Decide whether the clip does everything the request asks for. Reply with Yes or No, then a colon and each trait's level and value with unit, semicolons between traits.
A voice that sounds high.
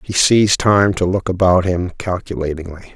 No: very low, 90 Hz